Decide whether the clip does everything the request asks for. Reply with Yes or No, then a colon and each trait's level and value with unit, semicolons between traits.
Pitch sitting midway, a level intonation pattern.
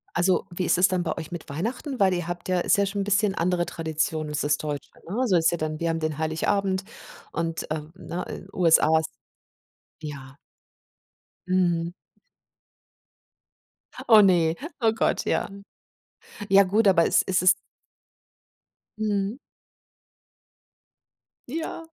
No: medium, 175 Hz; average, 3.6 semitones